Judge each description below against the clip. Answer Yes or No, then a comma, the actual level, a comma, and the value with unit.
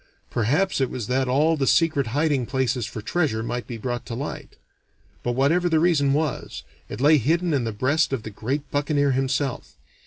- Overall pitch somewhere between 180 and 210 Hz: No, low, 135 Hz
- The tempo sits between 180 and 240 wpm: Yes, average, 190 wpm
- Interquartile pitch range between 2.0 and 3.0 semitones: No, average, 3.8 semitones